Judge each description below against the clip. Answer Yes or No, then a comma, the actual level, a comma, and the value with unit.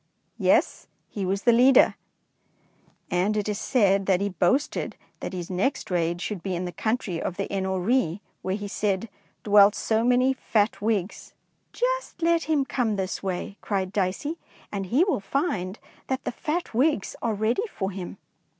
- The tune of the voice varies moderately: Yes, average, 4.9 semitones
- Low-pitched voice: No, high, 205 Hz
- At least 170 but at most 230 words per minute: Yes, average, 180 wpm